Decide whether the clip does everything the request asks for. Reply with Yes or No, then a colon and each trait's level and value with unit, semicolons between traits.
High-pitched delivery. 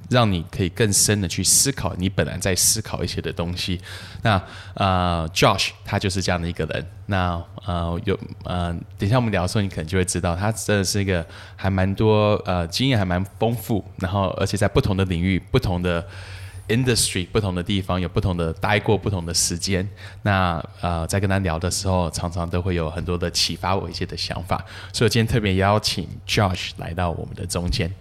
No: very low, 95 Hz